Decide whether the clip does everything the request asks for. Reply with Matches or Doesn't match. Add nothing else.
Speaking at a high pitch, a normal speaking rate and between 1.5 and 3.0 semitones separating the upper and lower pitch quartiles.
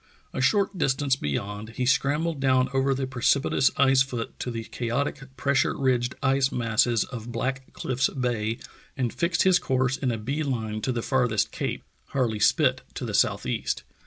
Doesn't match